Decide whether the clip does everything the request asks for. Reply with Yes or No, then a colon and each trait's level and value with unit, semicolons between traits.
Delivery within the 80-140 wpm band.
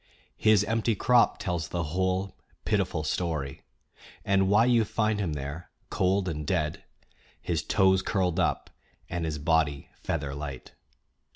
Yes: slow, 135 wpm